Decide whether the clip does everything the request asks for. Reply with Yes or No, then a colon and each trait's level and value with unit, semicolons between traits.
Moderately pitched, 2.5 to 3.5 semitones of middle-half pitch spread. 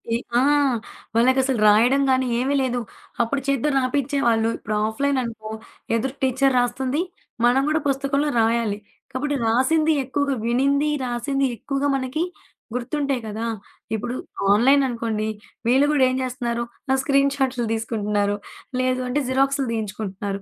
No: very high, 255 Hz; average, 3.1 semitones